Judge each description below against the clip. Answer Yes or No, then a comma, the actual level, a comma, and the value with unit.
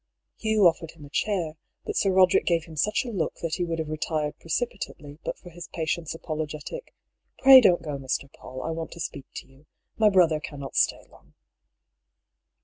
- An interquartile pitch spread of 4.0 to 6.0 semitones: No, average, 3.2 semitones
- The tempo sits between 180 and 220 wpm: Yes, average, 200 wpm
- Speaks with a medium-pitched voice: Yes, medium, 165 Hz